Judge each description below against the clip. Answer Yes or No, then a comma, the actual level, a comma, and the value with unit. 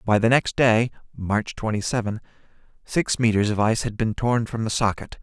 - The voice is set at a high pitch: No, low, 110 Hz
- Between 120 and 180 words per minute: No, average, 195 wpm